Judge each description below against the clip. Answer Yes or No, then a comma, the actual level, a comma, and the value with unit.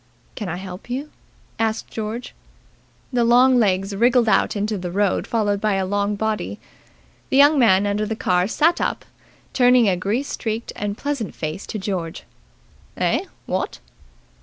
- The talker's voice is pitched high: Yes, high, 215 Hz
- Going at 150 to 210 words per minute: Yes, average, 160 wpm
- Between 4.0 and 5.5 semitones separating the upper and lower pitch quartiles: No, average, 3.6 semitones